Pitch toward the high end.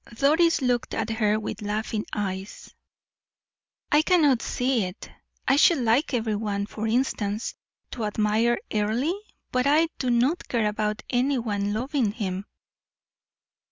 Yes: high, 230 Hz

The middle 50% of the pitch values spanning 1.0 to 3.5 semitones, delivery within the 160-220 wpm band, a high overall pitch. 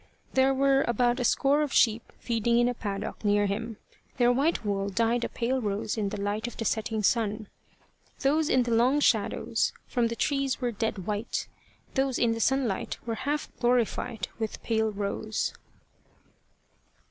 Yes: average, 3.2 semitones; average, 170 wpm; high, 230 Hz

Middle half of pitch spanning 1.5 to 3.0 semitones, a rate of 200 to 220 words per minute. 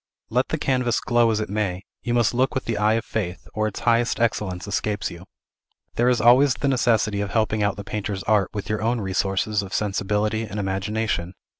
Yes: average, 2.7 semitones; fast, 205 wpm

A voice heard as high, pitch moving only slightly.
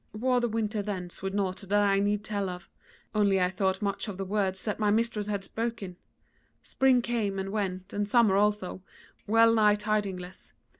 Yes: high, 205 Hz; narrow, 1.8 semitones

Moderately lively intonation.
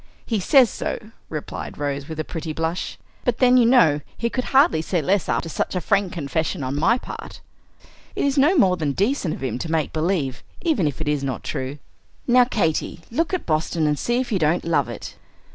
No: wide, 7.7 semitones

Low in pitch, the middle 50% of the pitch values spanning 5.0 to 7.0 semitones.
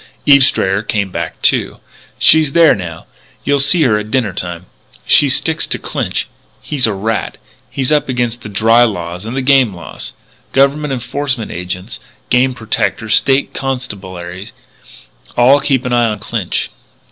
Yes: low, 120 Hz; average, 5.3 semitones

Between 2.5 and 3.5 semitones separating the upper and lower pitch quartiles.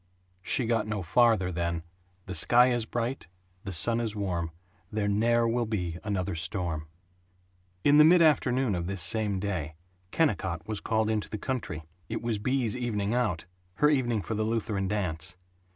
No: average, 4.6 semitones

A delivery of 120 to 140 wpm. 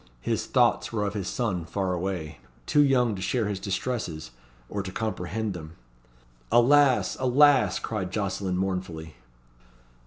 Yes: slow, 135 wpm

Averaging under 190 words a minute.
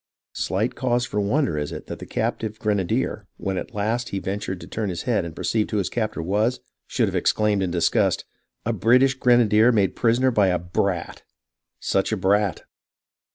No: average, 200 wpm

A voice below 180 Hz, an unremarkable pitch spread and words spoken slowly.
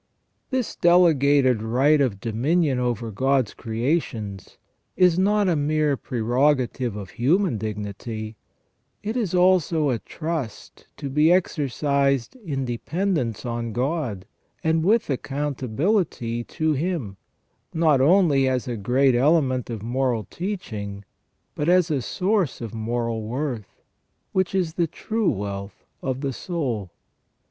No: low, 135 Hz; wide, 6.0 semitones; slow, 125 wpm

